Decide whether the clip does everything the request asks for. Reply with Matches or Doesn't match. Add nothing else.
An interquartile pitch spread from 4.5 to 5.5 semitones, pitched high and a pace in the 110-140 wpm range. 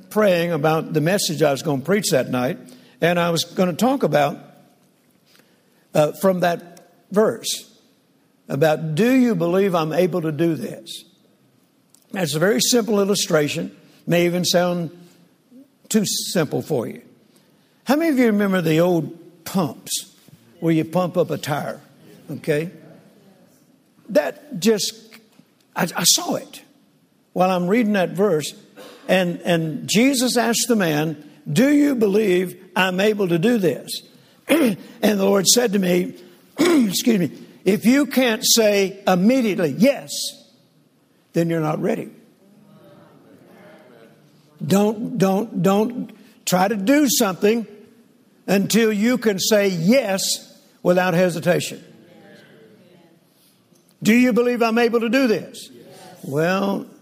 Matches